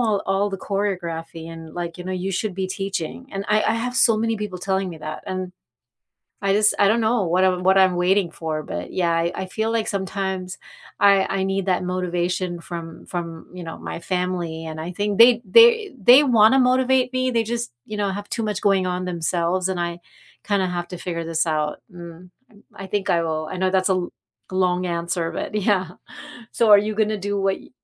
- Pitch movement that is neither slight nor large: Yes, average, 3.0 semitones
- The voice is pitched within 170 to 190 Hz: Yes, medium, 185 Hz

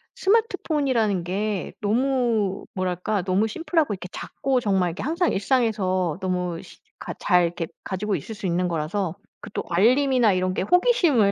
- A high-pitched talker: Yes, high, 205 Hz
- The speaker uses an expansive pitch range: Yes, wide, 5.9 semitones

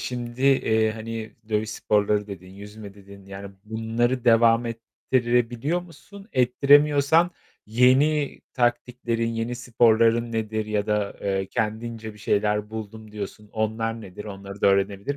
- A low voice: Yes, low, 110 Hz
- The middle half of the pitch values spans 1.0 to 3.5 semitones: Yes, narrow, 2.4 semitones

